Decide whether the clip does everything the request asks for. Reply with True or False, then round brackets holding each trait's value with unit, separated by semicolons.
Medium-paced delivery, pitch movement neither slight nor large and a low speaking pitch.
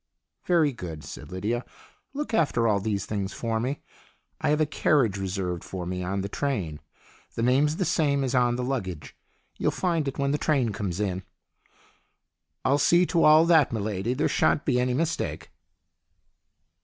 False (180 wpm; 7.0 semitones; 125 Hz)